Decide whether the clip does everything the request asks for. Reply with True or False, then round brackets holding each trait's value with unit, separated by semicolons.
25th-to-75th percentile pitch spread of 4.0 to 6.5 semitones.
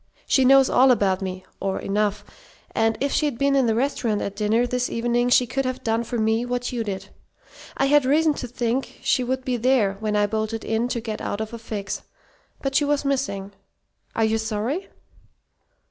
False (3.4 semitones)